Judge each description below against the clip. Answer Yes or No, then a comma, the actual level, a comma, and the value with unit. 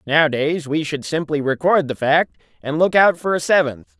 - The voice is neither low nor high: Yes, medium, 150 Hz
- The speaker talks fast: No, average, 195 wpm